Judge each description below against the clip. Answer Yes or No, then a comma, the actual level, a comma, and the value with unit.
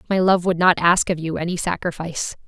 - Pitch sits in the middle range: Yes, medium, 175 Hz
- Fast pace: Yes, fast, 220 wpm